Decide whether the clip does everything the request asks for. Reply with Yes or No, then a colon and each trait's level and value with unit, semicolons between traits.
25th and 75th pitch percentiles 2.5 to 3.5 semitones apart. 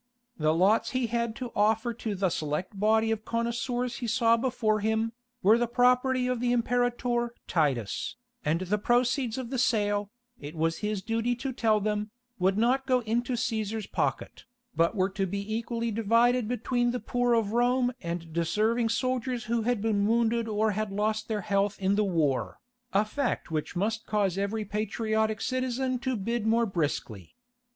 Yes: average, 3.1 semitones